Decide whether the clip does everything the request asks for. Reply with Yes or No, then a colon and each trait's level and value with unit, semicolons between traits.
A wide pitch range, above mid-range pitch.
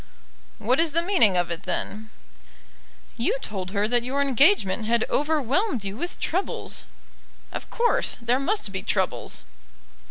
Yes: wide, 7.3 semitones; high, 245 Hz